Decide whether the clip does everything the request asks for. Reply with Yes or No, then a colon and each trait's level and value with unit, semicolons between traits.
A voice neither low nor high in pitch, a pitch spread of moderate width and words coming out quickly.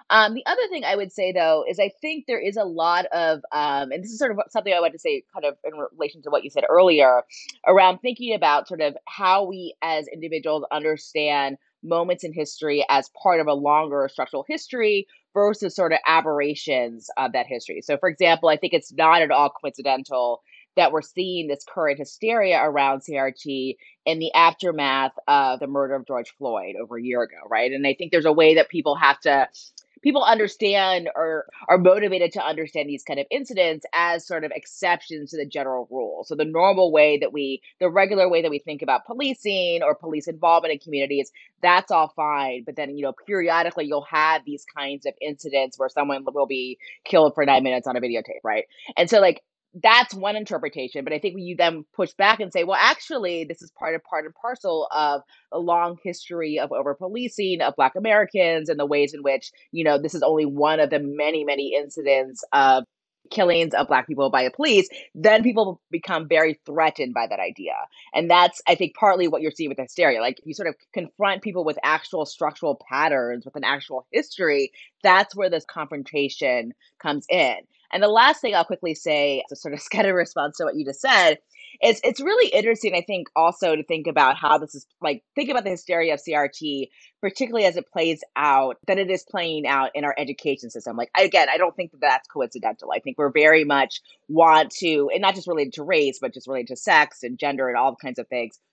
Yes: medium, 160 Hz; average, 4.6 semitones; fast, 215 wpm